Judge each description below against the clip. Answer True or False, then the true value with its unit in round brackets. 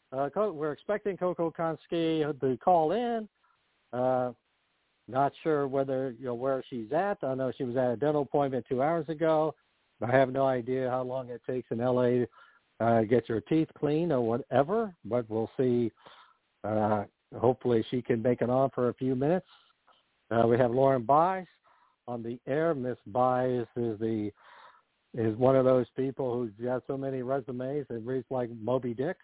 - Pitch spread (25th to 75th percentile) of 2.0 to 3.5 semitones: True (3.1 semitones)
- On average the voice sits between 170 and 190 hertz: False (130 Hz)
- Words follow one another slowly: False (180 wpm)